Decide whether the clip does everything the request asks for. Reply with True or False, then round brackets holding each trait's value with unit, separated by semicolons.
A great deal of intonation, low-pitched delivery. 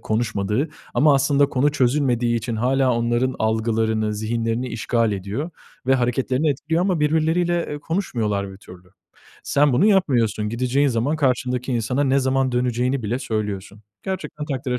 False (4.1 semitones; 125 Hz)